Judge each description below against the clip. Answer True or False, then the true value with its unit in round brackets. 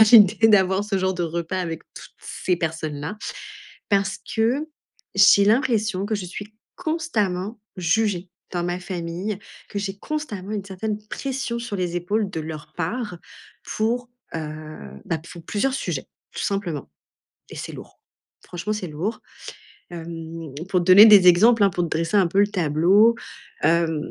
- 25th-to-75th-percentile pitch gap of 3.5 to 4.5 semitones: True (4.0 semitones)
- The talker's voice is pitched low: False (190 Hz)